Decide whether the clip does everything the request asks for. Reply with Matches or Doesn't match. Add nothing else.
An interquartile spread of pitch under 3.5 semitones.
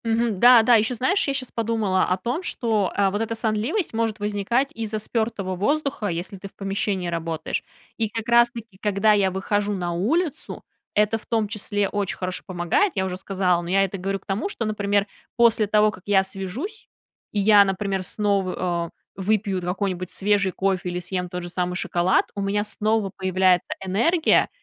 Matches